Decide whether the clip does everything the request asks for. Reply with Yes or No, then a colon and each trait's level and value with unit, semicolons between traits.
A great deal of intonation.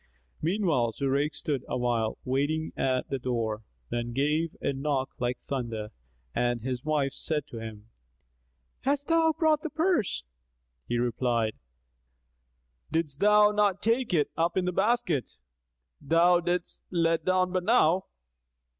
Yes: wide, 7.0 semitones